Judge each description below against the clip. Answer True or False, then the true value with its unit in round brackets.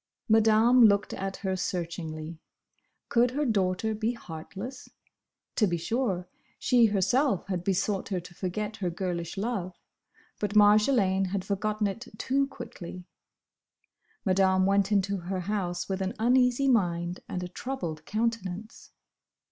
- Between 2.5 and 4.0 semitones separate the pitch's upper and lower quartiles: True (3.5 semitones)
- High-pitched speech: True (195 Hz)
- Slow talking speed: True (130 wpm)